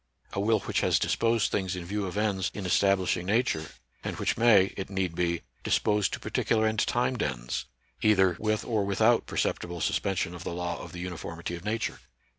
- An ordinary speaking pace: Yes, average, 190 wpm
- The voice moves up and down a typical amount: Yes, average, 3.5 semitones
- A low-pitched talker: Yes, very low, 95 Hz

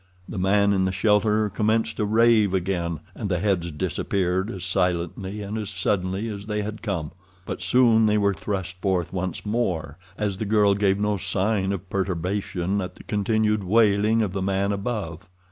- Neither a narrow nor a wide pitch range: No, narrow, 2.3 semitones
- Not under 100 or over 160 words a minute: No, average, 180 wpm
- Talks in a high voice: No, low, 100 Hz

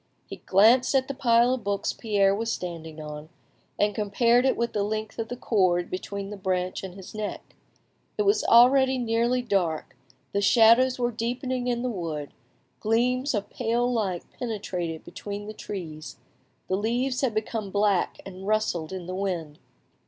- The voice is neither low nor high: No, high, 215 Hz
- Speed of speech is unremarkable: Yes, average, 165 wpm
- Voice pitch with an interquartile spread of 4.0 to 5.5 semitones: Yes, average, 4.3 semitones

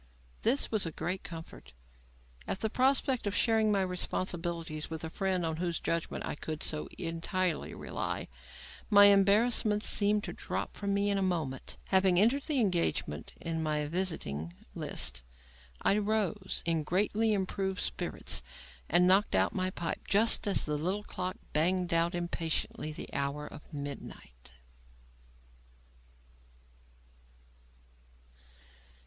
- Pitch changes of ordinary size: Yes, average, 4.0 semitones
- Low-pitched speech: No, medium, 180 Hz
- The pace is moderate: No, slow, 130 wpm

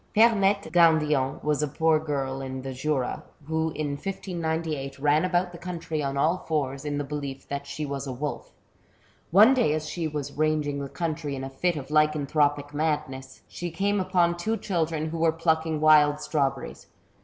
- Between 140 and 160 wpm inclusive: No, average, 180 wpm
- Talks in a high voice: No, medium, 155 Hz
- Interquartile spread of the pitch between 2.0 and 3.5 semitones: Yes, average, 2.7 semitones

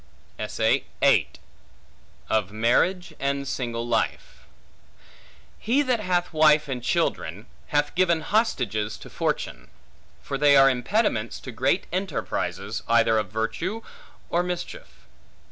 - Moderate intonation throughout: No, wide, 7.6 semitones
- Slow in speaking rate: Yes, slow, 110 wpm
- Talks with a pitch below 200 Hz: Yes, medium, 140 Hz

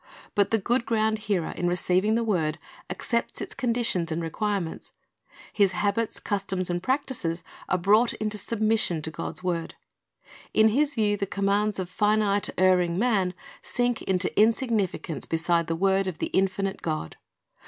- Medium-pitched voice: No, high, 200 Hz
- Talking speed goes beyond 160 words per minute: No, average, 155 wpm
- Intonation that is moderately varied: Yes, average, 3.5 semitones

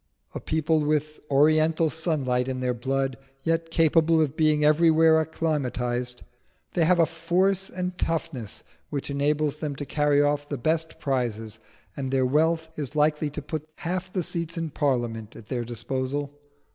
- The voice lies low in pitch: No, medium, 150 Hz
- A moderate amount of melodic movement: Yes, average, 3.4 semitones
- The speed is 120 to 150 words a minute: No, average, 160 wpm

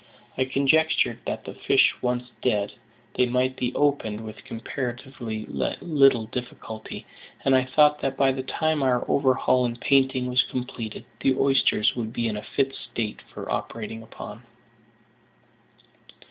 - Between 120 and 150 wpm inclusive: Yes, average, 145 wpm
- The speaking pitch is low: Yes, low, 125 Hz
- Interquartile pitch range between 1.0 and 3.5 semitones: Yes, average, 2.9 semitones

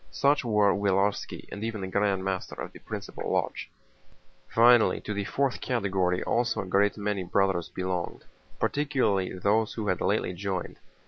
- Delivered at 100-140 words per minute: No, average, 155 wpm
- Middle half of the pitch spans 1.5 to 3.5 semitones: Yes, average, 2.9 semitones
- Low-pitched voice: Yes, low, 100 Hz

